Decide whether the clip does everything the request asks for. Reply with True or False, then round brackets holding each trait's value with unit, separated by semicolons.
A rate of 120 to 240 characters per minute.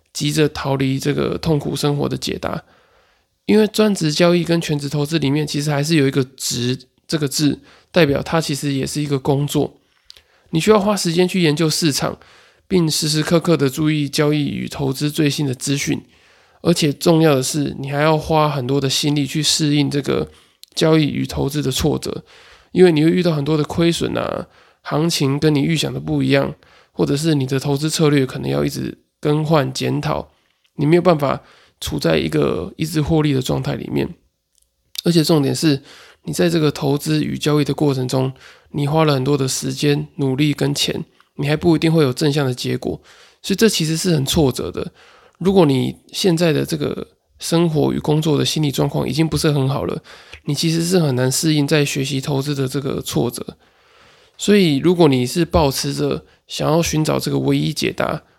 False (285 characters per minute)